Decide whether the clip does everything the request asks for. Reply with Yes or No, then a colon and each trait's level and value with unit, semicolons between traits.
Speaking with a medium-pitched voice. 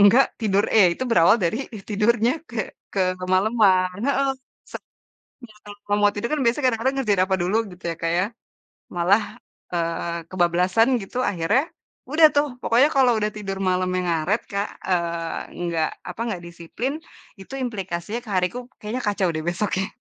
No: high, 200 Hz